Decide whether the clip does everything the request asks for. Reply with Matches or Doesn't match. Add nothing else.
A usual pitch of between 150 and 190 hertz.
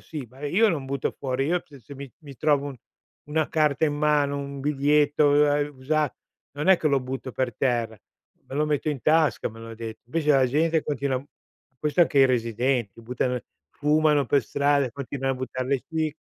Doesn't match